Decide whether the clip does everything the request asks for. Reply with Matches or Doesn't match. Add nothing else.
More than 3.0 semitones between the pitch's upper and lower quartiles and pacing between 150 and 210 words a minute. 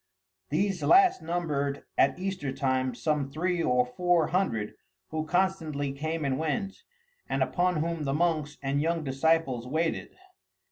Doesn't match